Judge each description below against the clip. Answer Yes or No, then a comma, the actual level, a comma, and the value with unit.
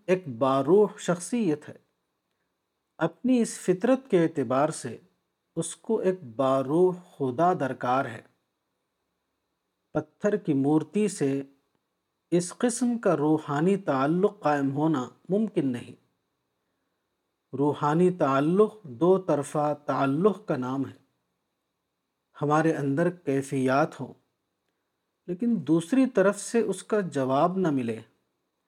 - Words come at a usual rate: No, slow, 105 wpm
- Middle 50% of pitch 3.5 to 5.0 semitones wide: No, wide, 5.6 semitones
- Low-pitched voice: No, medium, 160 Hz